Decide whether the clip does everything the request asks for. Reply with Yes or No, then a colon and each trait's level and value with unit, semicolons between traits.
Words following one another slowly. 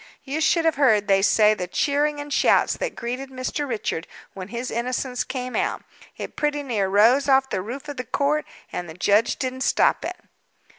No: average, 195 wpm